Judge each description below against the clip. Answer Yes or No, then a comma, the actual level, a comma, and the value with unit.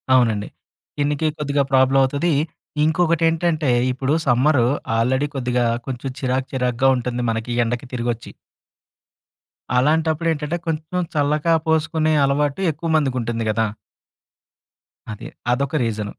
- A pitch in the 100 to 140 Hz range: Yes, low, 135 Hz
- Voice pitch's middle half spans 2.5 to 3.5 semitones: No, average, 4.0 semitones